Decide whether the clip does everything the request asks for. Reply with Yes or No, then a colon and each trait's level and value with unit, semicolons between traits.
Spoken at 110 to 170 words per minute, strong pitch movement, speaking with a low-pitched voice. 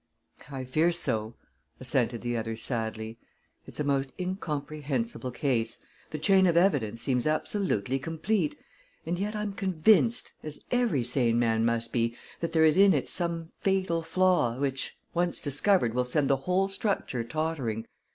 No: average, 150 wpm; wide, 7.1 semitones; medium, 150 Hz